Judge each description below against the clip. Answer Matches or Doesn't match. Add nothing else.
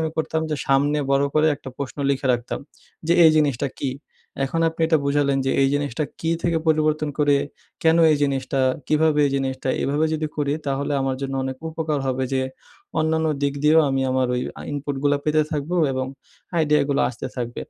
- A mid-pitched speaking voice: Matches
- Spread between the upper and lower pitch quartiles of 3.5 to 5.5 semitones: Doesn't match